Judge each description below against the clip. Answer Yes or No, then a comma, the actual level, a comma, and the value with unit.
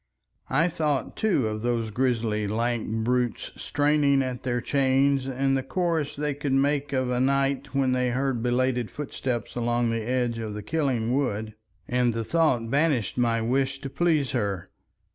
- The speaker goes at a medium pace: Yes, average, 165 wpm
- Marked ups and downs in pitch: No, average, 3.0 semitones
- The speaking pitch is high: No, low, 130 Hz